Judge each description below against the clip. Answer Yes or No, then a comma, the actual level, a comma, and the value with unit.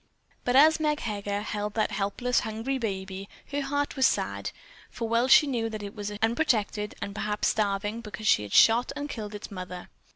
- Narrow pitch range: No, average, 3.4 semitones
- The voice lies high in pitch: Yes, high, 220 Hz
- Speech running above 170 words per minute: Yes, average, 190 wpm